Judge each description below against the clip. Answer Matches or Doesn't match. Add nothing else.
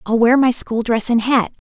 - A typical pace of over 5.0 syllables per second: Doesn't match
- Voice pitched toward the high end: Matches